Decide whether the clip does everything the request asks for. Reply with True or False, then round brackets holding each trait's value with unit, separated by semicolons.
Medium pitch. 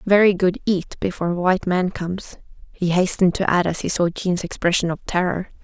True (180 Hz)